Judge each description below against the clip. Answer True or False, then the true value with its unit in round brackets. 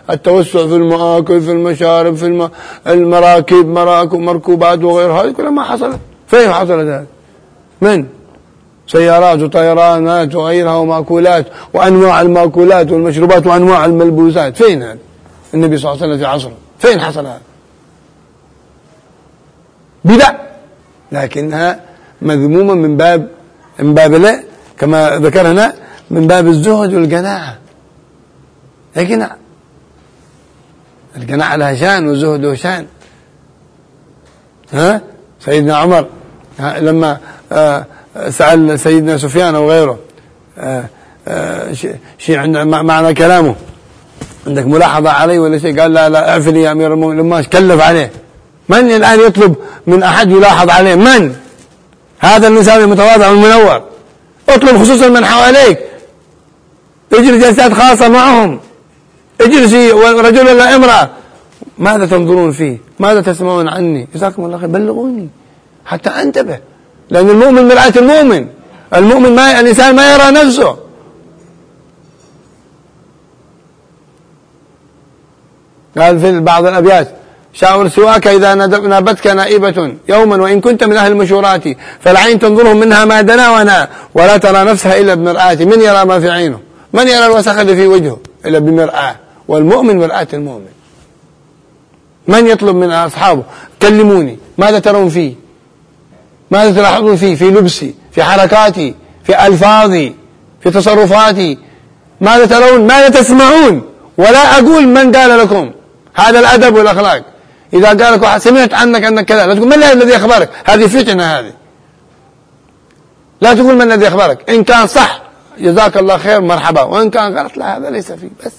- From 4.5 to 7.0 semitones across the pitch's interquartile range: True (5.1 semitones)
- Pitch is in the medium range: True (180 Hz)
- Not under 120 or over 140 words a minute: True (125 wpm)